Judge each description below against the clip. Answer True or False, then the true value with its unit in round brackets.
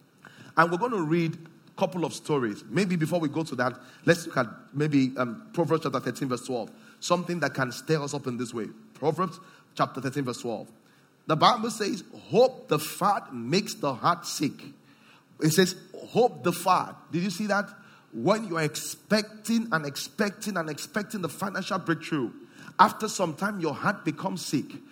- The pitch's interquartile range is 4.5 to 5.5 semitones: True (5.2 semitones)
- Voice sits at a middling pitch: True (165 Hz)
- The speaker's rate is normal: True (180 wpm)